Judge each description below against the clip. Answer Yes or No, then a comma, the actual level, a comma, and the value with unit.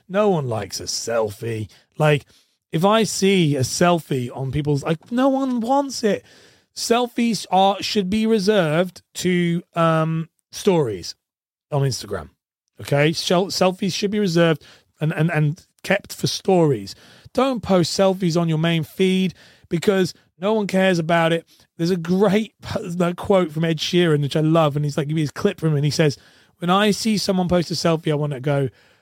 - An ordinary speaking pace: Yes, average, 175 wpm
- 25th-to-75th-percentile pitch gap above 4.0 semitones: Yes, average, 4.6 semitones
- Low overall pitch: No, medium, 170 Hz